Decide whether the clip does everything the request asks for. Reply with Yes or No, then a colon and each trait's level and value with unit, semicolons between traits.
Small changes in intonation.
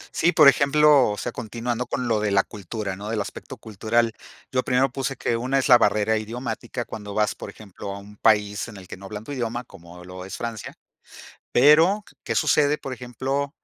No: average, 4.1 semitones